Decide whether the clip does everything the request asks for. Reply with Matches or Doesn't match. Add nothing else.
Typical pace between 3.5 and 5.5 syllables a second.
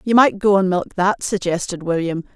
Matches